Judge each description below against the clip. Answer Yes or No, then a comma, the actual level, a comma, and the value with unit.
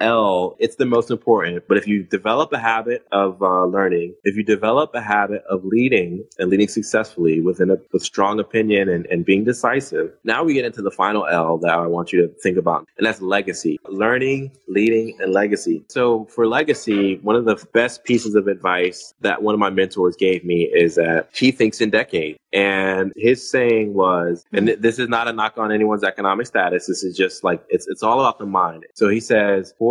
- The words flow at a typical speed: No, fast, 210 wpm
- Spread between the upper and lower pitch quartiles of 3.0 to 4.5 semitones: Yes, average, 3.5 semitones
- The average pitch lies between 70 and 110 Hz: Yes, low, 105 Hz